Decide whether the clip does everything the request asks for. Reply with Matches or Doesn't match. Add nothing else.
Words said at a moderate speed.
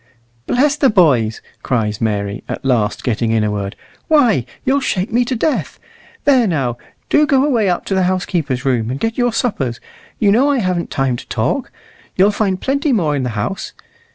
Matches